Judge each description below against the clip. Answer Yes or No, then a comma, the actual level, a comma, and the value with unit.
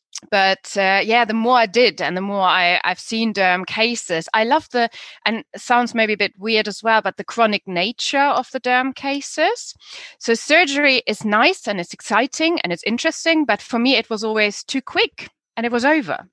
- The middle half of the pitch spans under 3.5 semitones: No, average, 4.4 semitones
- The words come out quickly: Yes, fast, 210 wpm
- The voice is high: Yes, high, 225 Hz